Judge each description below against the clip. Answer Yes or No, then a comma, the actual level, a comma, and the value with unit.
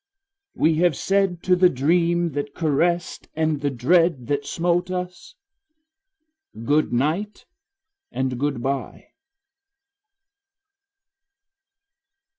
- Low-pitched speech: No, medium, 160 Hz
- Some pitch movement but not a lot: Yes, average, 3.8 semitones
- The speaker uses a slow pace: Yes, slow, 80 wpm